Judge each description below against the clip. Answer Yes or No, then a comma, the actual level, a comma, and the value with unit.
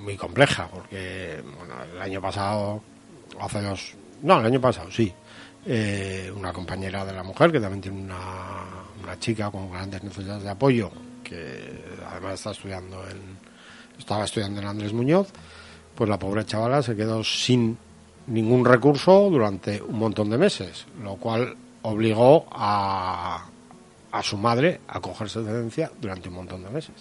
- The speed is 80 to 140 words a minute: No, average, 160 wpm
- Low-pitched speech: Yes, low, 100 Hz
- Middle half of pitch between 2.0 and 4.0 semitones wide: Yes, average, 3.5 semitones